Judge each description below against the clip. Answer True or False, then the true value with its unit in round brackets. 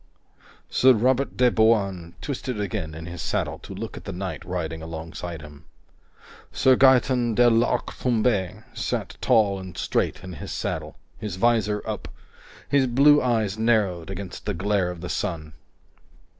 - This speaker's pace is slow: False (155 wpm)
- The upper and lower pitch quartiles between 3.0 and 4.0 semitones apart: False (5.3 semitones)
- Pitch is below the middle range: True (105 Hz)